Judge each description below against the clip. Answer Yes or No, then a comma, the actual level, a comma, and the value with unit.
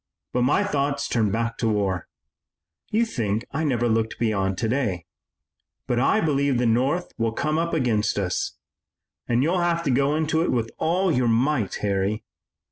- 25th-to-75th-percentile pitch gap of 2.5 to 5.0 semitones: No, wide, 5.4 semitones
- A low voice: Yes, low, 125 Hz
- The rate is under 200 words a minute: Yes, average, 170 wpm